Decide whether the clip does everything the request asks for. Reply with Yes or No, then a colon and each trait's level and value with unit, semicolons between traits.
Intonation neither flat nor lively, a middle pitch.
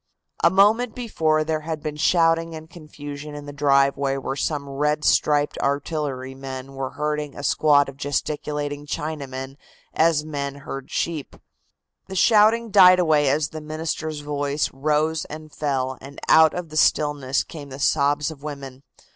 No: narrow, 2.0 semitones; medium, 150 Hz